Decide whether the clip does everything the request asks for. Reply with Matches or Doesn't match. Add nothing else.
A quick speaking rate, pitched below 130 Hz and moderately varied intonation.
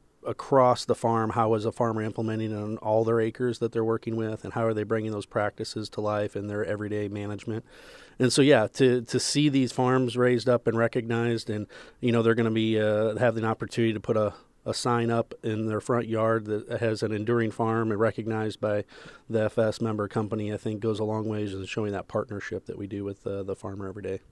Doesn't match